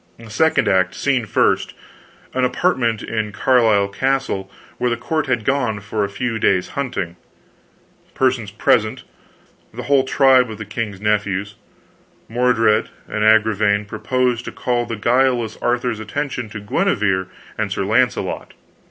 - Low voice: Yes, low, 110 Hz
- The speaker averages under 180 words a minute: Yes, slow, 135 wpm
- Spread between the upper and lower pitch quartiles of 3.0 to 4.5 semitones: Yes, average, 3.4 semitones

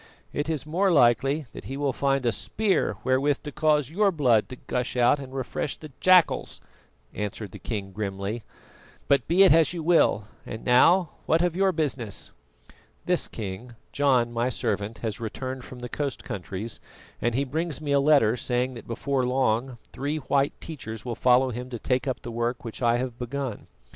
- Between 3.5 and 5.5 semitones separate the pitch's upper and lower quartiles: Yes, average, 3.8 semitones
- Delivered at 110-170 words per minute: No, average, 185 wpm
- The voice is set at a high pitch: No, low, 130 Hz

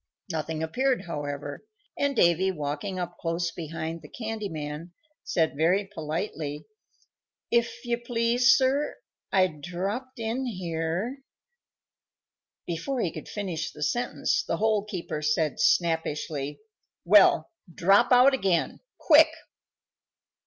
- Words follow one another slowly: Yes, slow, 115 wpm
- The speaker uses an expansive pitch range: Yes, wide, 6.3 semitones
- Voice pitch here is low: No, medium, 180 Hz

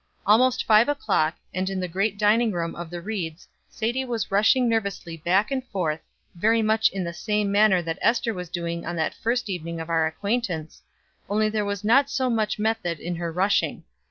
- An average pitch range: Yes, average, 4.6 semitones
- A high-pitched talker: Yes, high, 200 Hz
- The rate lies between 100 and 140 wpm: No, average, 195 wpm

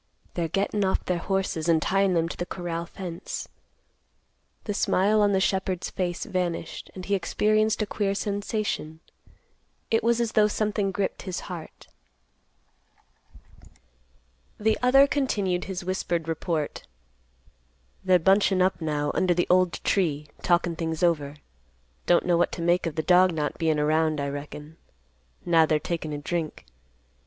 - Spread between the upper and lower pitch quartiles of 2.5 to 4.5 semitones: Yes, average, 3.3 semitones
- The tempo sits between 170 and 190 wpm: No, average, 150 wpm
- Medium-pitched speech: Yes, medium, 180 Hz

